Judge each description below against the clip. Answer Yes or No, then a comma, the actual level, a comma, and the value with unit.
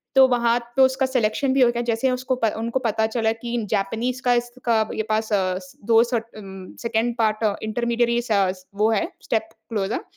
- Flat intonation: Yes, narrow, 2.2 semitones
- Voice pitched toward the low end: No, high, 230 Hz